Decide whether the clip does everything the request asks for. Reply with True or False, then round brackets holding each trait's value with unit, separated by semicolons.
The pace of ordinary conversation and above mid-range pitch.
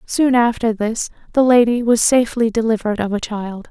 True (180 wpm; 230 Hz)